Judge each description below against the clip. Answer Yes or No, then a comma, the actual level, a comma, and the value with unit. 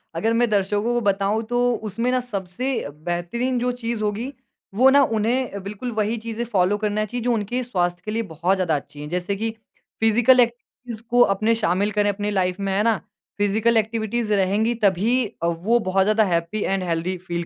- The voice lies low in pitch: No, high, 210 Hz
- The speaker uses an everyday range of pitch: Yes, average, 3.7 semitones